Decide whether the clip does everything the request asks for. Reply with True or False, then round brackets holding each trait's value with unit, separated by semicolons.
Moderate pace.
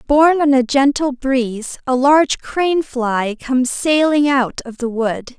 True (165 wpm)